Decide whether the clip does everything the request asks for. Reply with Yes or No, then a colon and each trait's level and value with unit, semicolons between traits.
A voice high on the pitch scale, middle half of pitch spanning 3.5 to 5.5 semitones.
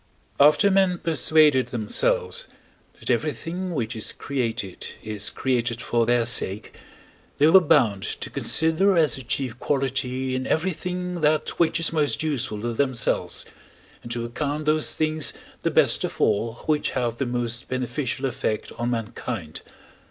No: low, 130 Hz; average, 5.0 semitones